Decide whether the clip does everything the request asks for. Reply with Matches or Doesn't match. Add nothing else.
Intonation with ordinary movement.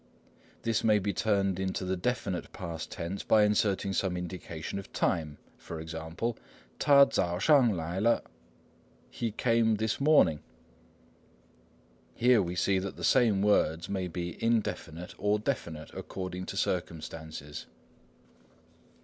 Matches